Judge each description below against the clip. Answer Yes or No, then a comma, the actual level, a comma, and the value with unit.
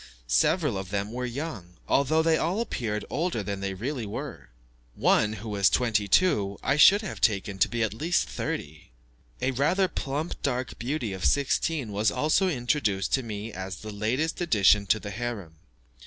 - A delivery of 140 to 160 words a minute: No, average, 175 wpm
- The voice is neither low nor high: No, low, 115 Hz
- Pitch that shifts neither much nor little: No, wide, 6.6 semitones